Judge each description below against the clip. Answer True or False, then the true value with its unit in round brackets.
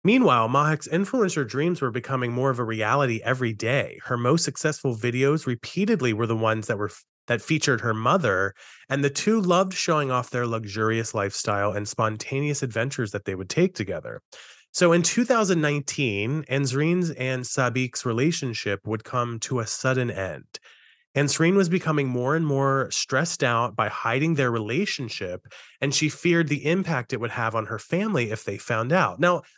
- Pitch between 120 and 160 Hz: True (135 Hz)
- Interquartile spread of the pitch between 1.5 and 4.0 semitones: False (5.1 semitones)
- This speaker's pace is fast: False (170 wpm)